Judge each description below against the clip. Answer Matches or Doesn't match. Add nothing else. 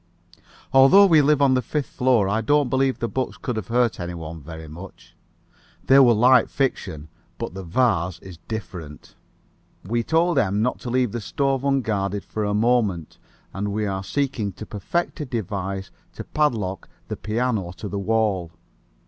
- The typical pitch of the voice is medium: Doesn't match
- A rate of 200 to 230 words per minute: Doesn't match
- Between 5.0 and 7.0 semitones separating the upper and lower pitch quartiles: Matches